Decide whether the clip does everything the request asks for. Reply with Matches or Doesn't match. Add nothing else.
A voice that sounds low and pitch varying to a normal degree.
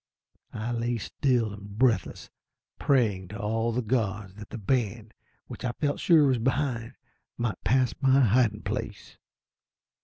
Matches